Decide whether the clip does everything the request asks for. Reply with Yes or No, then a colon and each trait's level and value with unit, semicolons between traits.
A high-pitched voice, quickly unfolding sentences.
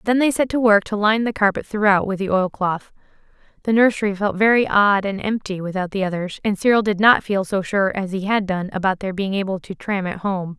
Yes: high, 200 Hz; fast, 245 wpm